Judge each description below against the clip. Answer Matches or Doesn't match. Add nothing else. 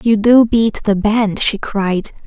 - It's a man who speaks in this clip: Doesn't match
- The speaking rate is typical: Matches